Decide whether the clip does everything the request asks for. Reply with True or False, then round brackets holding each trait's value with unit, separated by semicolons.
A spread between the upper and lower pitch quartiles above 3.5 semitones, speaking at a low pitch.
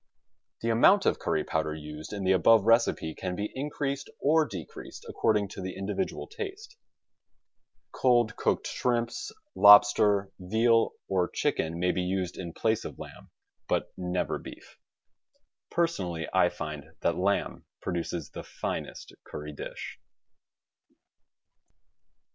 True (4.9 semitones; 100 Hz)